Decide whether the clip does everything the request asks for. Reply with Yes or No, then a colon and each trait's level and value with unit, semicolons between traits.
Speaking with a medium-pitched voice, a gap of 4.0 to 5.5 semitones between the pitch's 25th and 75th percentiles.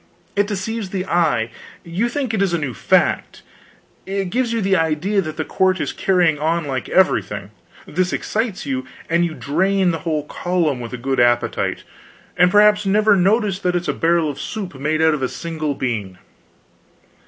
Yes: medium, 170 Hz; average, 4.8 semitones